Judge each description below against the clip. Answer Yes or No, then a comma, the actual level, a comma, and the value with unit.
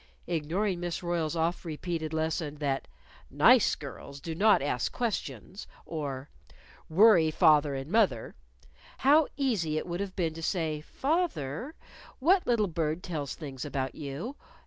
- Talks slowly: No, average, 145 wpm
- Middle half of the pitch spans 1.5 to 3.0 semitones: No, average, 5.1 semitones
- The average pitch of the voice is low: No, medium, 165 Hz